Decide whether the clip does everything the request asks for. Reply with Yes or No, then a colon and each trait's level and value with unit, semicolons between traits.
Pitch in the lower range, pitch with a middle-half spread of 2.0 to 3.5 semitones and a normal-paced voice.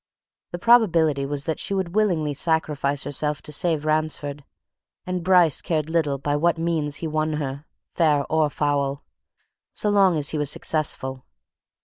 No: medium, 155 Hz; average, 2.7 semitones; average, 155 wpm